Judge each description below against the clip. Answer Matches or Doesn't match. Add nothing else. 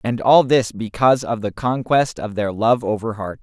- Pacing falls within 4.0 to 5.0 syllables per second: Matches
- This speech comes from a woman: Doesn't match